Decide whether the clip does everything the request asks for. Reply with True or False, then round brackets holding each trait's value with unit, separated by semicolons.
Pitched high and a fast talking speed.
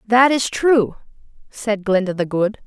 False (220 Hz; 160 wpm)